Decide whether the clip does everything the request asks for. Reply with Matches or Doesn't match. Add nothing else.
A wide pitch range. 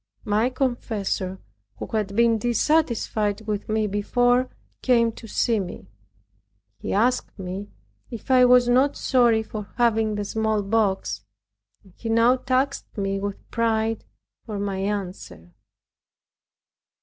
Doesn't match